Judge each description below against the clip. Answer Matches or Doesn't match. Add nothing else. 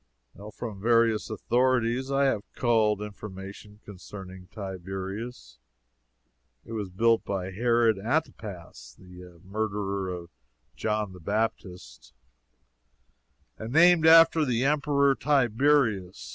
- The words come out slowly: Matches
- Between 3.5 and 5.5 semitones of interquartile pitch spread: Matches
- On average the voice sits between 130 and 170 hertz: Doesn't match